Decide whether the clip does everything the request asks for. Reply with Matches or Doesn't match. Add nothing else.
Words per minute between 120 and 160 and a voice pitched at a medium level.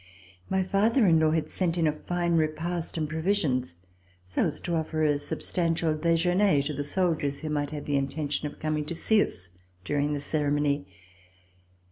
Doesn't match